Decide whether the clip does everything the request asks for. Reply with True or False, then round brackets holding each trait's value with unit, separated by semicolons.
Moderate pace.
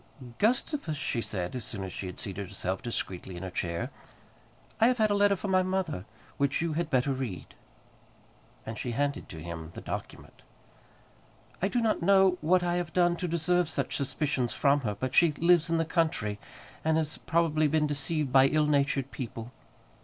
True (190 wpm)